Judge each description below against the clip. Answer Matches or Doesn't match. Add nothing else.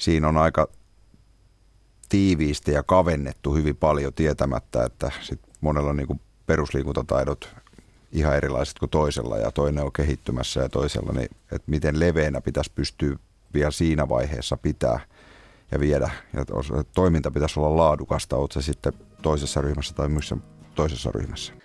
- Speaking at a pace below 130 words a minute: Doesn't match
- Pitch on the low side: Matches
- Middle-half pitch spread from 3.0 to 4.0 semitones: Doesn't match